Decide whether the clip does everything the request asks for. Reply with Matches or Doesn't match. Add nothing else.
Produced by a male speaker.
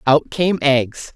Doesn't match